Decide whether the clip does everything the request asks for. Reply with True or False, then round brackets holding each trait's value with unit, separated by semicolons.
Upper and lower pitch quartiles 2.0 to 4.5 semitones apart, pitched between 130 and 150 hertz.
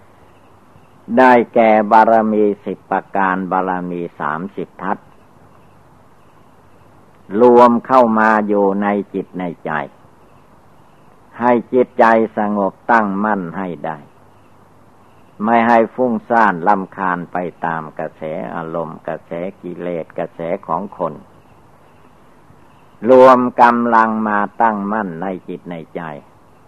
False (3.8 semitones; 105 Hz)